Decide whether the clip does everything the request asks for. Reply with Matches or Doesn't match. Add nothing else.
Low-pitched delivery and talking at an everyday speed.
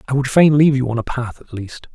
Doesn't match